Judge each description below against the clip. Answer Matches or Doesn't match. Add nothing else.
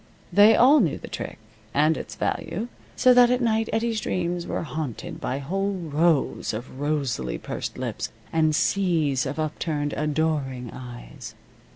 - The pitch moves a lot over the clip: Matches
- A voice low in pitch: Doesn't match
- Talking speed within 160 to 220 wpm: Doesn't match